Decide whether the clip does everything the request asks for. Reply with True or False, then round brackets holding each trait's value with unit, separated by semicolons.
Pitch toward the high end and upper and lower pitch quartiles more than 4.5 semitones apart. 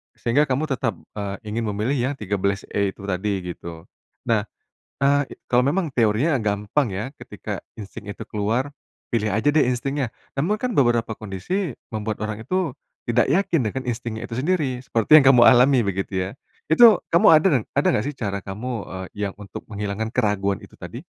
False (115 Hz; 5.1 semitones)